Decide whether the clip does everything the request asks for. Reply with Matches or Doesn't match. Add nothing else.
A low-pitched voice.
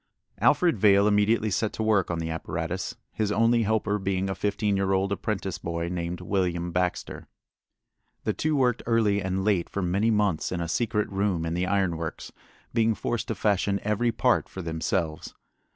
Matches